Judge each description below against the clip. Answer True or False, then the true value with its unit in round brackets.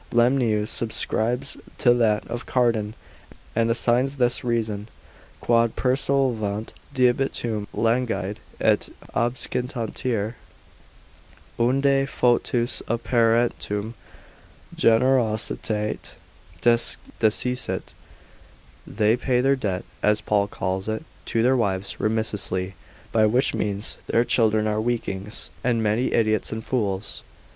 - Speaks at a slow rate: True (100 wpm)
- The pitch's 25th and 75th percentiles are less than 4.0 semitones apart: True (2.5 semitones)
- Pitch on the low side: True (115 Hz)